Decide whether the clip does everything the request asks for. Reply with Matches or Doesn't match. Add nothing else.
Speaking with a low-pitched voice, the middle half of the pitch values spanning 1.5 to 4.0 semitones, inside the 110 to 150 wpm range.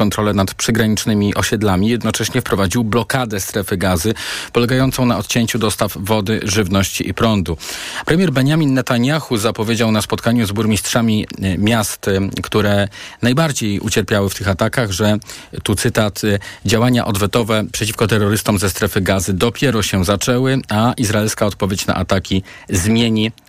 Matches